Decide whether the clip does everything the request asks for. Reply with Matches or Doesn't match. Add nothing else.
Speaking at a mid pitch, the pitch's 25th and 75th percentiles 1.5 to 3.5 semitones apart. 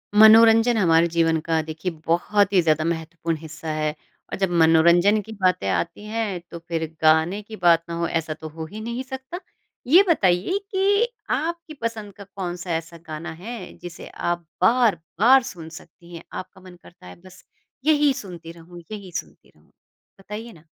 Doesn't match